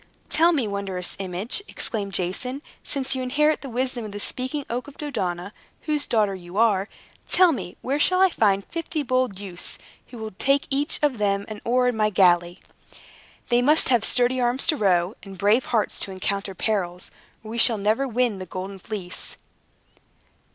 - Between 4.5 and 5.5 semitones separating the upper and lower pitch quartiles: Yes, average, 4.9 semitones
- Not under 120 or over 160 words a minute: No, average, 180 wpm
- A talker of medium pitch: No, high, 220 Hz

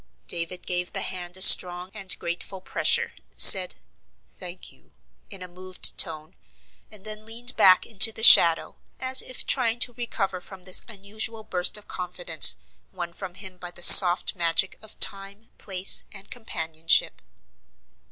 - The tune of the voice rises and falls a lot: No, average, 3.2 semitones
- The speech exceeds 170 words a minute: No, average, 150 wpm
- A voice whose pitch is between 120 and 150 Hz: No, medium, 185 Hz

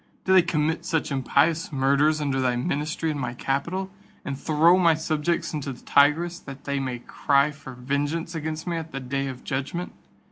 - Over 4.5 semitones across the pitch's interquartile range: No, average, 3.1 semitones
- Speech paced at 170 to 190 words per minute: Yes, average, 185 wpm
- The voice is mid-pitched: Yes, medium, 150 Hz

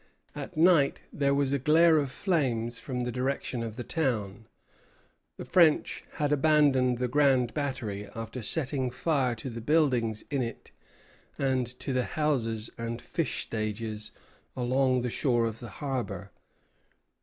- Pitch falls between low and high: No, low, 130 Hz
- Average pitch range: Yes, average, 3.6 semitones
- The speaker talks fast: No, average, 145 wpm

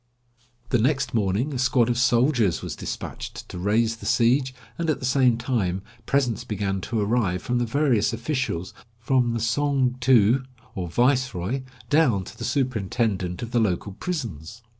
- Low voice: Yes, low, 120 Hz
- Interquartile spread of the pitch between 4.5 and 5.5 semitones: No, average, 4.1 semitones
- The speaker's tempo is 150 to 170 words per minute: Yes, average, 160 wpm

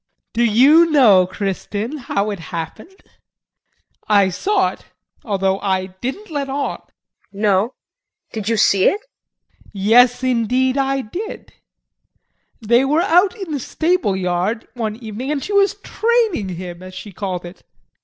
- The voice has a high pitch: Yes, high, 235 Hz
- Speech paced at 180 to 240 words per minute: No, average, 145 wpm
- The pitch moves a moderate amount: No, wide, 7.4 semitones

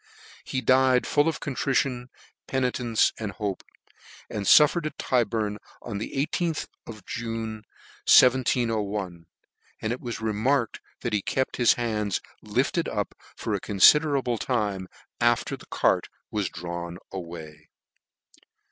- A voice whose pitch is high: No, low, 115 Hz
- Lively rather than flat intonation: No, average, 4.0 semitones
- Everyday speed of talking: No, slow, 130 wpm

